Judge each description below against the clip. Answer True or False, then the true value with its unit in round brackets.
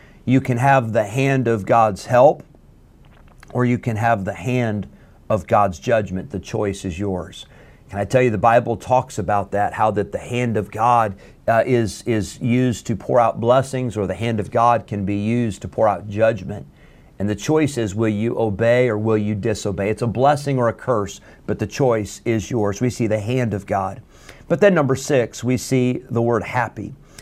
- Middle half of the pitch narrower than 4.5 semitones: True (3.3 semitones)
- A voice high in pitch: False (115 Hz)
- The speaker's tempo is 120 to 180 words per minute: False (205 wpm)